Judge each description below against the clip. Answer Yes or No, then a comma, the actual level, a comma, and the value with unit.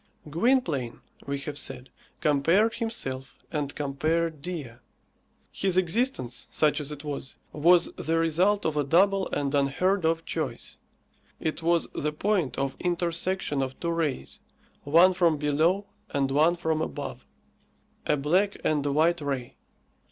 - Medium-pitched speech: Yes, medium, 160 Hz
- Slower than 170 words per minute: Yes, average, 140 wpm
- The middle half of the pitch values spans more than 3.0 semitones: Yes, average, 3.7 semitones